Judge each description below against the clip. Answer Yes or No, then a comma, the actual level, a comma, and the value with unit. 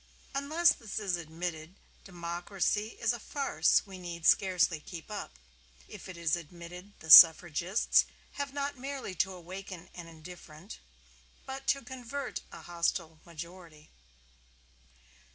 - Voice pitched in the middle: Yes, medium, 180 Hz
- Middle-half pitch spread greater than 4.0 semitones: Yes, average, 4.5 semitones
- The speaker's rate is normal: No, slow, 125 wpm